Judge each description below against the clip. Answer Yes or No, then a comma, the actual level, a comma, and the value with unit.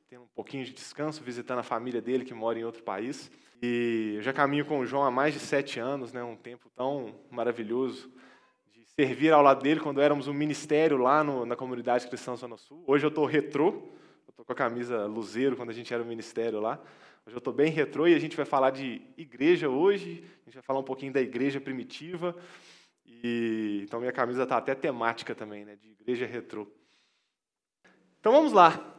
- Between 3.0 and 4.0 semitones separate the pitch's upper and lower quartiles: Yes, average, 3.4 semitones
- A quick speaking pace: Yes, fast, 205 wpm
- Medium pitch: No, low, 130 Hz